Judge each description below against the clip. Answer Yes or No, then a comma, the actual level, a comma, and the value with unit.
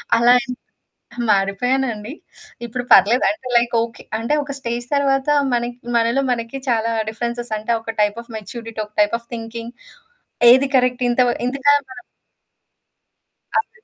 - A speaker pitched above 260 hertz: No, high, 240 Hz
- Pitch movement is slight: Yes, narrow, 1.9 semitones